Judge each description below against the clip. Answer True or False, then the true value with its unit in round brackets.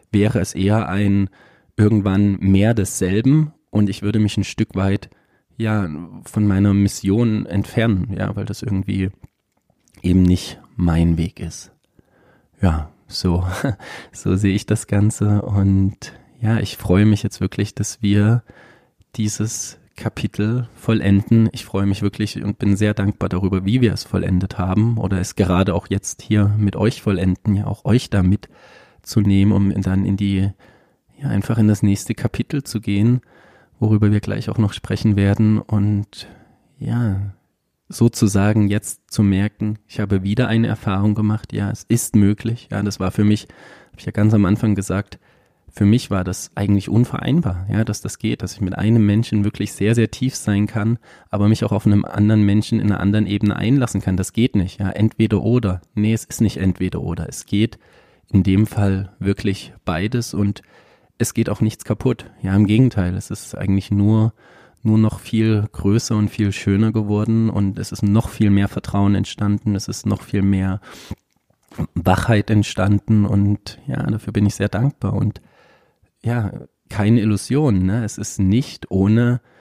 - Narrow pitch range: True (1.8 semitones)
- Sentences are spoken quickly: False (170 wpm)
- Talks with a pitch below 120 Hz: True (105 Hz)